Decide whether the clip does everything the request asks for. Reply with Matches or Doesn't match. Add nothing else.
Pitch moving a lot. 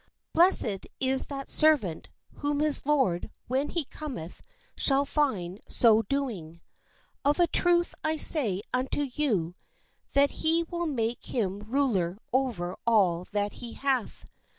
Matches